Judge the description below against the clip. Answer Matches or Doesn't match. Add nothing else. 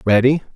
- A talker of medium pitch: Doesn't match